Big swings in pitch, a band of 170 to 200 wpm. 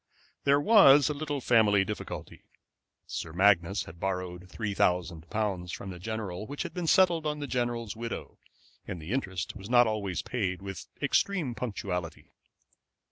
No: wide, 6.4 semitones; average, 155 wpm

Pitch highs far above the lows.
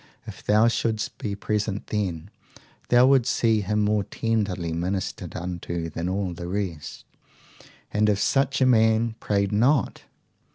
No: average, 3.5 semitones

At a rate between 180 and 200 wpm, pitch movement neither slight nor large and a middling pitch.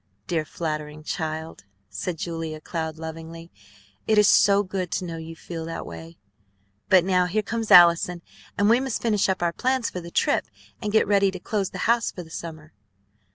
Yes: average, 190 wpm; average, 3.7 semitones; medium, 170 Hz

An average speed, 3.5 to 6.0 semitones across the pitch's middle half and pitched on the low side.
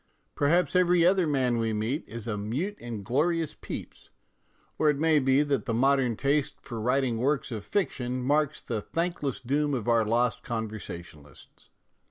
Yes: average, 165 wpm; average, 4.6 semitones; low, 130 Hz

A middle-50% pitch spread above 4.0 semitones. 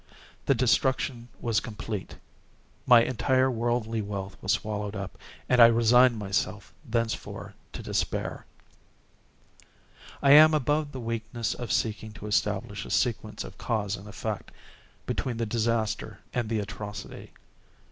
No: narrow, 2.6 semitones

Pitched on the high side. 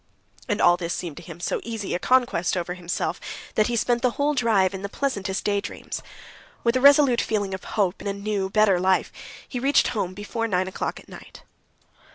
Yes: high, 205 Hz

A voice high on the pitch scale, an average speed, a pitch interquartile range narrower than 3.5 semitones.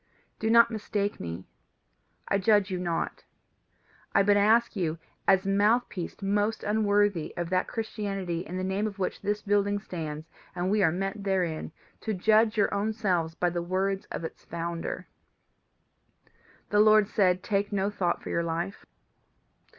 Yes: high, 195 Hz; average, 160 wpm; average, 2.8 semitones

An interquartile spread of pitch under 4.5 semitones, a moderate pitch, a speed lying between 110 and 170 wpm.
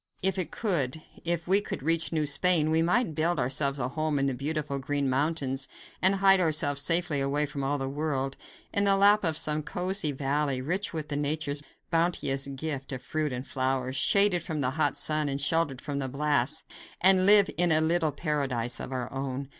No: average, 3.5 semitones; medium, 150 Hz; average, 195 wpm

